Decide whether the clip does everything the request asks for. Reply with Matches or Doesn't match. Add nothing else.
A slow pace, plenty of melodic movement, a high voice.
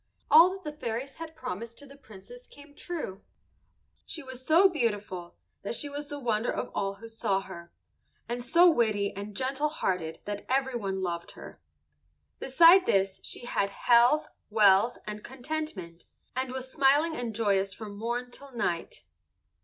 Doesn't match